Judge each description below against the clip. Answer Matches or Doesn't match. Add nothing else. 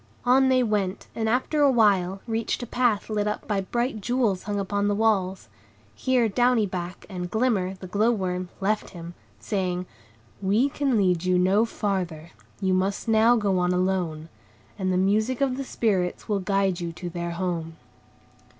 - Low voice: Doesn't match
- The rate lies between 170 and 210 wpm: Matches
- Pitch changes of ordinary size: Matches